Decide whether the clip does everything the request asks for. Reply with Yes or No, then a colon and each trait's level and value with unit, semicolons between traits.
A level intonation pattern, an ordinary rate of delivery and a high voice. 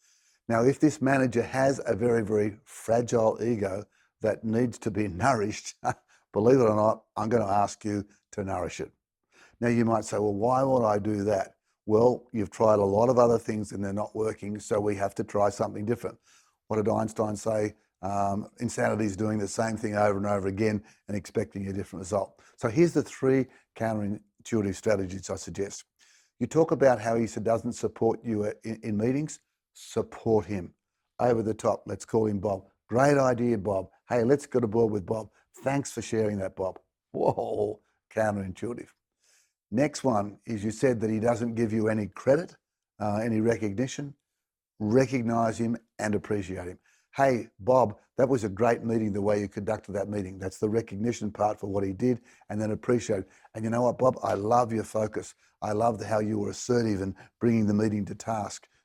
No: narrow, 2.3 semitones; average, 190 wpm; low, 110 Hz